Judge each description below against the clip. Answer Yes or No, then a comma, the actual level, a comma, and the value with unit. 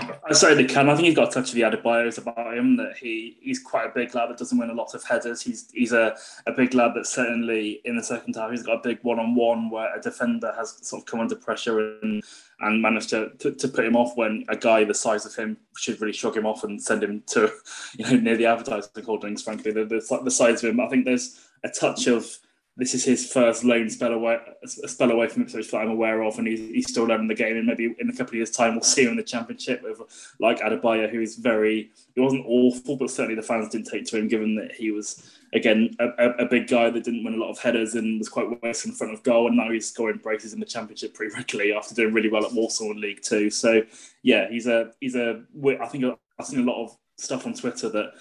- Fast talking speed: Yes, fast, 270 wpm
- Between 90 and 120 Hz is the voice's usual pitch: Yes, low, 115 Hz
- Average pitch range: No, narrow, 1.9 semitones